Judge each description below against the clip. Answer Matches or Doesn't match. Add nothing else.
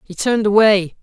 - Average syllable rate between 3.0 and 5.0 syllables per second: Doesn't match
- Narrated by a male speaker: Matches